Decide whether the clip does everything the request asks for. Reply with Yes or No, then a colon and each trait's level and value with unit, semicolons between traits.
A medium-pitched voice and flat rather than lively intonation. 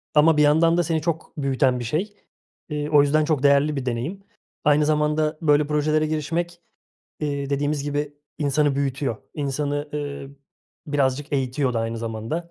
Yes: medium, 145 Hz; narrow, 1.8 semitones